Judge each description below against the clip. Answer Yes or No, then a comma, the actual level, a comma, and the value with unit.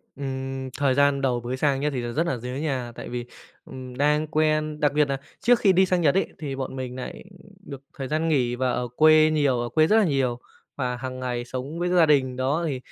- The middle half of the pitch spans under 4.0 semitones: Yes, average, 3.2 semitones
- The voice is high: No, low, 135 Hz